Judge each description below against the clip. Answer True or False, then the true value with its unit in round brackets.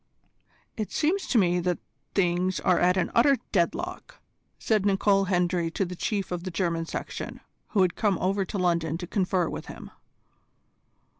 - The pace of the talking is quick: False (165 wpm)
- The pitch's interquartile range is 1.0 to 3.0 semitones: True (2.4 semitones)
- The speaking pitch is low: False (185 Hz)